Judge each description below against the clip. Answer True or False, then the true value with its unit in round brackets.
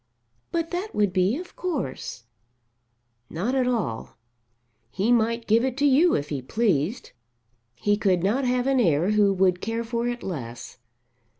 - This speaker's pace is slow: False (160 wpm)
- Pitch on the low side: False (225 Hz)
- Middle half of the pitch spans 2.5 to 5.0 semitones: False (5.6 semitones)